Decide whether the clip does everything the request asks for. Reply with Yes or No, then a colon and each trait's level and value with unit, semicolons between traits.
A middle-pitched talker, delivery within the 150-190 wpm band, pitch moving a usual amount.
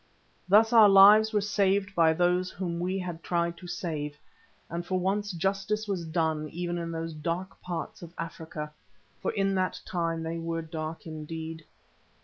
Yes: medium, 175 Hz; average, 165 wpm; average, 3.0 semitones